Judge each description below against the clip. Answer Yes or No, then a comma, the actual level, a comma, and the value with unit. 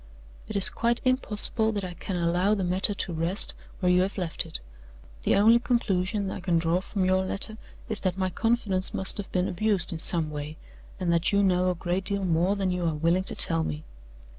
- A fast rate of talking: Yes, fast, 215 wpm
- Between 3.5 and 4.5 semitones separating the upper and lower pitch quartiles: No, narrow, 2.6 semitones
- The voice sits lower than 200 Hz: Yes, medium, 185 Hz